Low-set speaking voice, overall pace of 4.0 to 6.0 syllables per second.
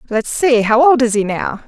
No: high, 240 Hz; 4.9 syllables/s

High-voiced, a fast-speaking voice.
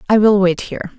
Yes: high, 200 Hz; fast, 245 wpm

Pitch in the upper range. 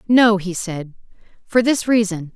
Yes: high, 205 Hz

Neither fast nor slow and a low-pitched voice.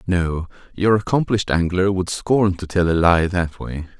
Yes: average, 180 wpm; very low, 90 Hz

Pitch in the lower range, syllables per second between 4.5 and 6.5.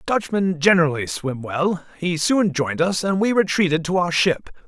No: medium, 175 Hz; 5.0 syllables/s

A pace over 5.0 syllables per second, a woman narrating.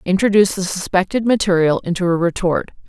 Yes: 6.1 syllables/s; female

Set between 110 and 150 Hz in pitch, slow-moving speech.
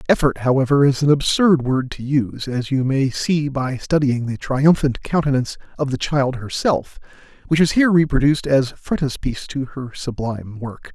No: low, 135 Hz; average, 170 wpm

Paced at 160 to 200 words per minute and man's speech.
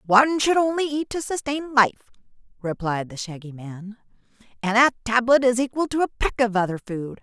No: average, 185 wpm; female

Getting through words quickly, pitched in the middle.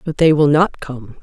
Yes: fast, 245 wpm; medium, 145 Hz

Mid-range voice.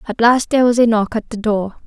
No: high, 225 Hz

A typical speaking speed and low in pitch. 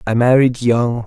Yes: average, 170 wpm; low, 120 Hz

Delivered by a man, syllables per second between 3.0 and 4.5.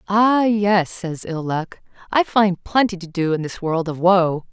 No: female; 4.0 syllables/s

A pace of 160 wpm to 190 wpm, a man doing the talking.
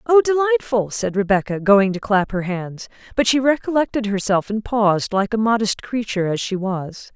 No: average, 185 wpm; female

